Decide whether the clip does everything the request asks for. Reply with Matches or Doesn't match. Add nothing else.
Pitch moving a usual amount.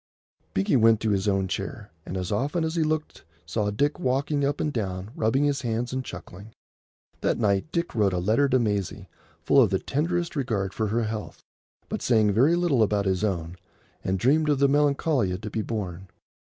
Doesn't match